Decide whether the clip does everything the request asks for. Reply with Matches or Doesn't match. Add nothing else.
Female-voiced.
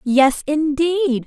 Matches